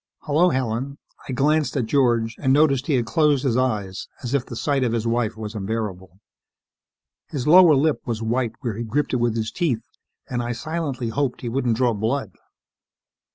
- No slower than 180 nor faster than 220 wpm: Yes, average, 190 wpm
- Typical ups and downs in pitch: Yes, average, 3.7 semitones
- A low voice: Yes, low, 125 Hz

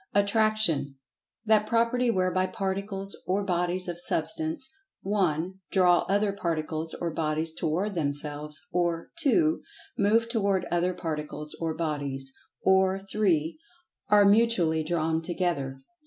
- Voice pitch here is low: No, medium, 180 Hz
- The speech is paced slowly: Yes, slow, 115 wpm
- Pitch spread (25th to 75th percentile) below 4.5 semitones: Yes, average, 4.1 semitones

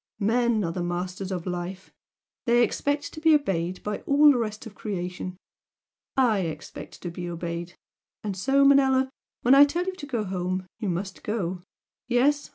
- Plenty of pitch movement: Yes, wide, 6.8 semitones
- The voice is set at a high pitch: Yes, high, 210 Hz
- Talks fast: No, average, 170 wpm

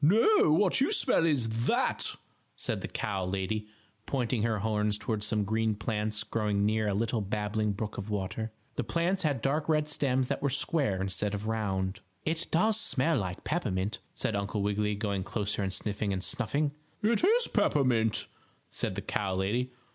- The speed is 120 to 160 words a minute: No, average, 175 wpm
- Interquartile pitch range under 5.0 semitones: No, wide, 5.6 semitones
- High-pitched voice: No, low, 110 Hz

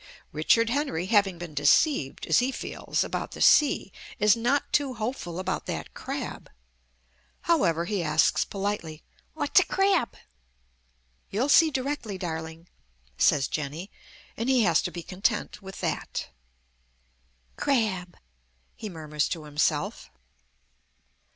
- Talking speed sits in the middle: No, slow, 125 wpm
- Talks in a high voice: Yes, high, 195 Hz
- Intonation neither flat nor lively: No, wide, 7.1 semitones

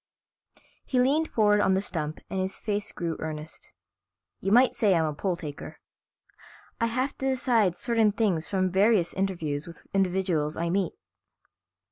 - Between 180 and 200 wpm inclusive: No, average, 155 wpm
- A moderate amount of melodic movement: Yes, average, 4.8 semitones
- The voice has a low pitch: No, high, 190 Hz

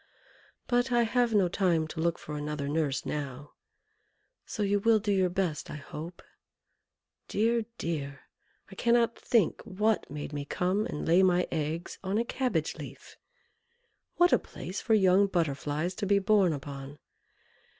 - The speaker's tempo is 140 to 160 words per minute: Yes, average, 155 wpm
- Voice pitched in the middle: Yes, medium, 180 Hz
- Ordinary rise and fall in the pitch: No, wide, 6.0 semitones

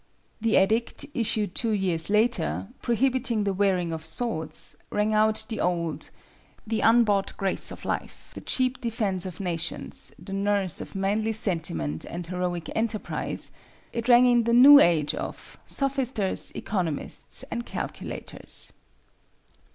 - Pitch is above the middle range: Yes, high, 210 Hz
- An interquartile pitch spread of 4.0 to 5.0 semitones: Yes, average, 4.5 semitones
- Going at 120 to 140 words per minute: Yes, slow, 135 wpm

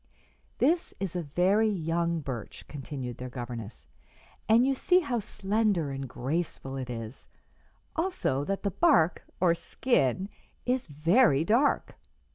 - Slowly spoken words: Yes, slow, 130 wpm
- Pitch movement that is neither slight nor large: No, wide, 8.6 semitones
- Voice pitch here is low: No, medium, 170 Hz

